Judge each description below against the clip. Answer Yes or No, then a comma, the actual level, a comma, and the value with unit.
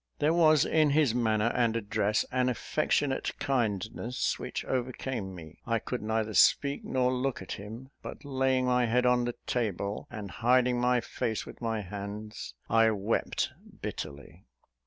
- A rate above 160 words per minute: No, average, 155 wpm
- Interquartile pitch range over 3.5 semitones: No, average, 3.2 semitones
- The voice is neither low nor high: No, low, 120 Hz